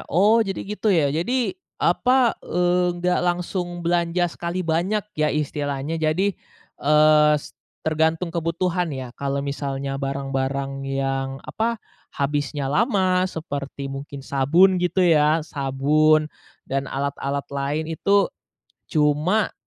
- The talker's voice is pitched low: No, medium, 155 Hz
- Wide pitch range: No, average, 4.3 semitones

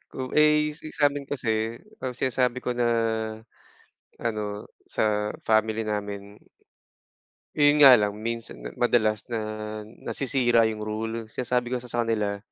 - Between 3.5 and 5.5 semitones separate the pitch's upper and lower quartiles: No, average, 3.0 semitones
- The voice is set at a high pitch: No, low, 115 Hz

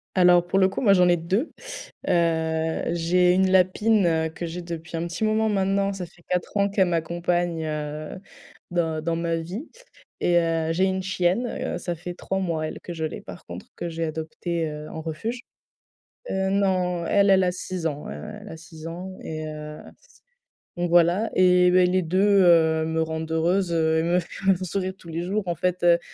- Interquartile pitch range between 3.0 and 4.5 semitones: No, narrow, 2.5 semitones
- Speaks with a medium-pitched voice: Yes, medium, 175 Hz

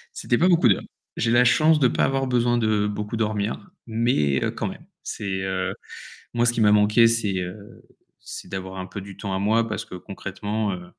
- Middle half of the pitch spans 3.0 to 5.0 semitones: Yes, average, 3.5 semitones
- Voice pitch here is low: Yes, low, 105 Hz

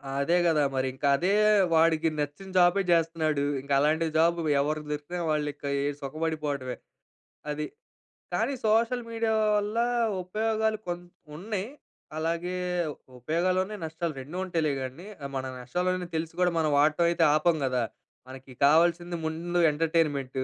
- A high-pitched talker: No, medium, 165 Hz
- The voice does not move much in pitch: No, average, 3.2 semitones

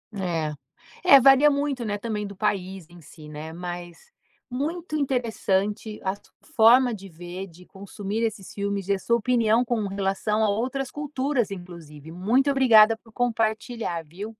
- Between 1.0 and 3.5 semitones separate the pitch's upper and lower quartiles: No, average, 4.6 semitones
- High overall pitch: Yes, high, 210 Hz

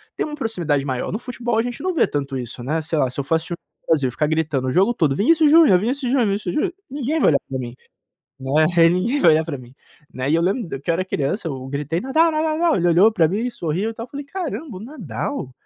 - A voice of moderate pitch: Yes, medium, 175 Hz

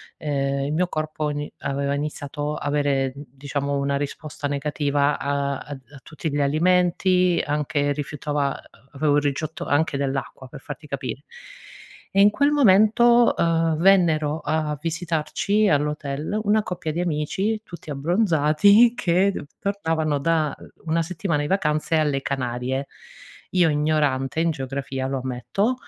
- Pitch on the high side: No, medium, 150 Hz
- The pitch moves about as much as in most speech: Yes, average, 3.2 semitones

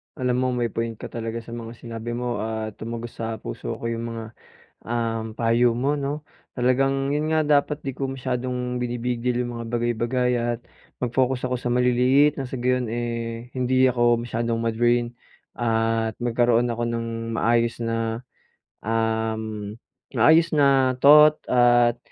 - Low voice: Yes, low, 120 Hz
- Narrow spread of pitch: Yes, narrow, 1.7 semitones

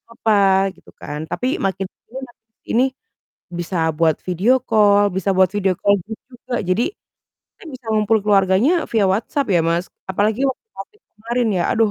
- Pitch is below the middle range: No, high, 210 Hz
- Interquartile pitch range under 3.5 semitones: No, average, 3.8 semitones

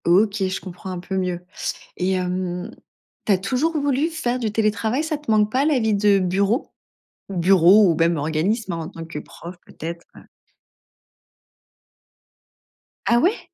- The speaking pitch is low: No, high, 195 Hz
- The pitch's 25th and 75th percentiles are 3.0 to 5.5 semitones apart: Yes, average, 4.3 semitones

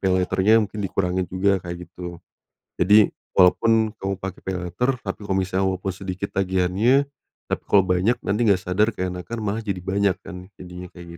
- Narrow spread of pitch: Yes, narrow, 2.0 semitones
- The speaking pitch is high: No, very low, 95 Hz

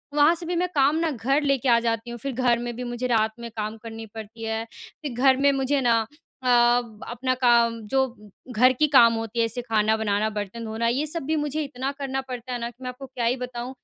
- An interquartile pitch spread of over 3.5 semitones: No, average, 2.8 semitones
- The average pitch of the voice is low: No, high, 240 Hz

